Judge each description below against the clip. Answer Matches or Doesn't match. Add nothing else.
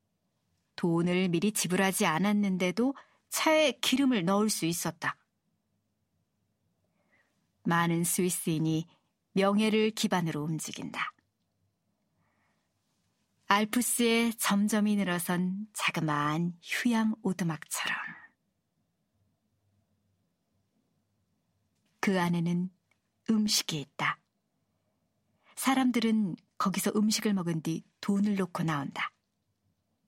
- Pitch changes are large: Doesn't match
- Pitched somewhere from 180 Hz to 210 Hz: Matches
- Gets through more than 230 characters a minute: Doesn't match